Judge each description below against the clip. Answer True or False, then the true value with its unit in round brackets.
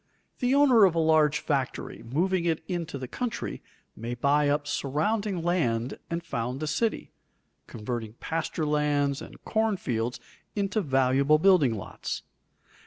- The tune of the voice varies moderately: False (5.7 semitones)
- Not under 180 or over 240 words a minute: False (140 wpm)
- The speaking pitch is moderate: True (150 Hz)